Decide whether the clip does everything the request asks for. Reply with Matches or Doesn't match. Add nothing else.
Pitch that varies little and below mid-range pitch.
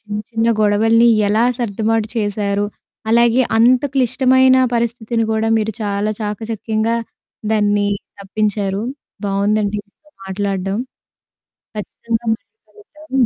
Doesn't match